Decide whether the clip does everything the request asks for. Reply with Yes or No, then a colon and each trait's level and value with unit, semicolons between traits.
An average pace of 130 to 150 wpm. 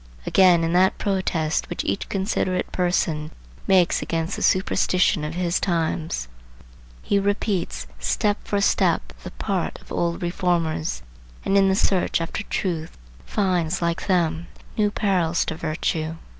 Yes: average, 140 wpm